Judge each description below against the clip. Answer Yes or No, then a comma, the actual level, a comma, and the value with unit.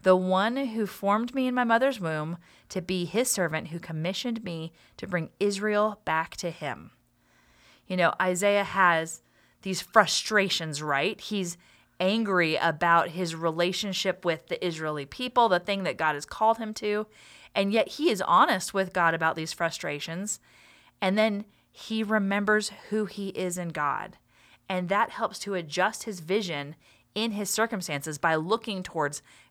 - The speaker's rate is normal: Yes, average, 160 wpm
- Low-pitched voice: No, medium, 185 Hz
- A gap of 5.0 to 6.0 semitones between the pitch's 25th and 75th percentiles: No, average, 4.2 semitones